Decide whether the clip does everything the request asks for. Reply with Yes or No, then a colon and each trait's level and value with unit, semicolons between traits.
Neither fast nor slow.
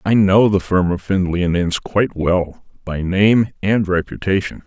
Yes: average, 180 wpm